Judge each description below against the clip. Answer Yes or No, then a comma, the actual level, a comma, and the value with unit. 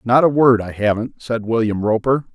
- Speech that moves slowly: No, fast, 205 wpm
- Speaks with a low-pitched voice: Yes, low, 115 Hz